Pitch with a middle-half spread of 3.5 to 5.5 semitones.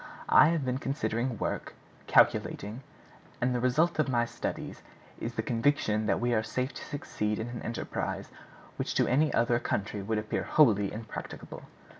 No: average, 3.1 semitones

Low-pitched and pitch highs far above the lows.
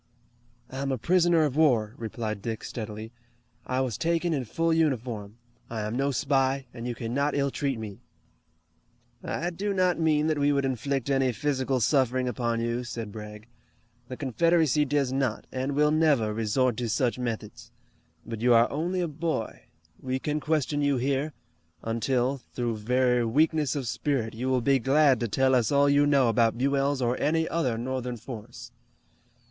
No: low, 130 Hz; average, 3.7 semitones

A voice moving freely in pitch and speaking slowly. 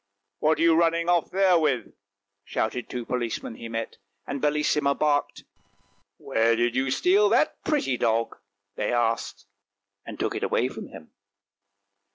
No: wide, 6.0 semitones; average, 170 wpm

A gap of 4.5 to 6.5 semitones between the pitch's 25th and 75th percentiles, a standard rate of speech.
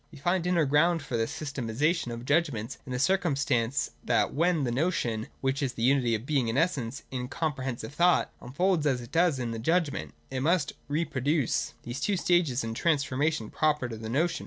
No: average, 5.0 semitones; fast, 210 wpm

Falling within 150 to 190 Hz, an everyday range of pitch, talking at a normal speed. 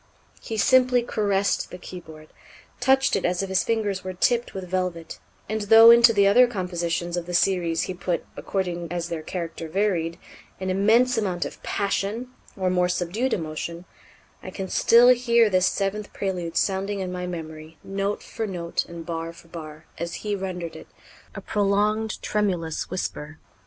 Yes: medium, 185 Hz; average, 3.6 semitones; average, 165 wpm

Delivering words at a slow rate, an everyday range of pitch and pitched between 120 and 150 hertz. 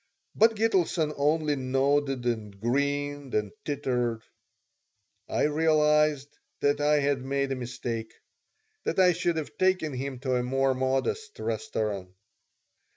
Yes: slow, 125 wpm; average, 3.3 semitones; medium, 140 Hz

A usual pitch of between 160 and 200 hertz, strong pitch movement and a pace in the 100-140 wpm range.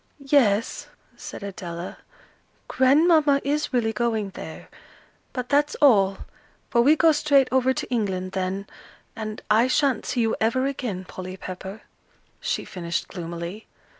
No: high, 225 Hz; wide, 6.1 semitones; slow, 135 wpm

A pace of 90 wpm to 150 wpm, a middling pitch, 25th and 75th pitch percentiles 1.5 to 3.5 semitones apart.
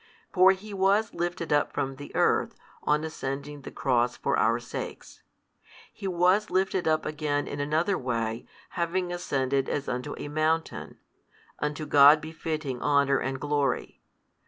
No: average, 145 wpm; medium, 150 Hz; average, 4.0 semitones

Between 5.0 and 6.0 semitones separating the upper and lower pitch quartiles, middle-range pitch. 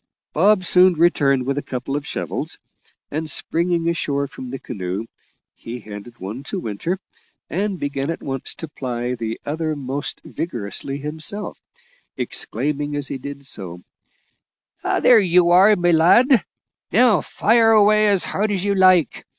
Yes: wide, 5.6 semitones; medium, 155 Hz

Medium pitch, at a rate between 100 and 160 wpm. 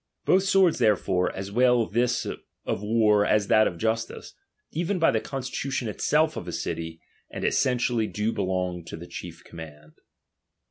No: low, 110 Hz; average, 155 wpm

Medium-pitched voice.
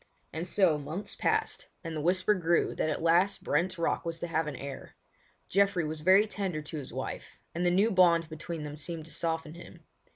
Yes: medium, 165 Hz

